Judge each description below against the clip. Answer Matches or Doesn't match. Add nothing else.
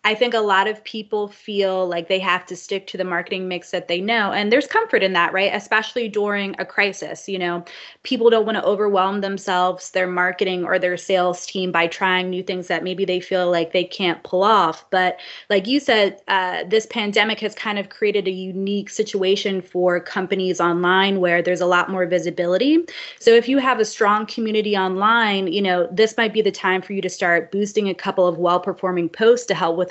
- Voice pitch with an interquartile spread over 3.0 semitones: Doesn't match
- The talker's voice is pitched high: Matches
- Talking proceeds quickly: Matches